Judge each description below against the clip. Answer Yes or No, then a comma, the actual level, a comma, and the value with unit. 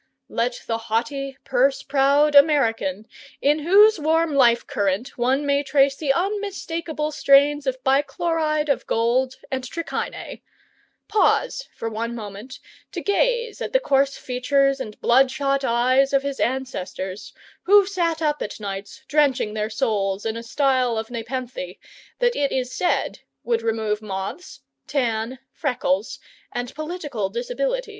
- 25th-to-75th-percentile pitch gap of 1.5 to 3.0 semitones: No, average, 4.6 semitones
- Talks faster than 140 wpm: No, slow, 135 wpm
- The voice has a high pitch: Yes, very high, 270 Hz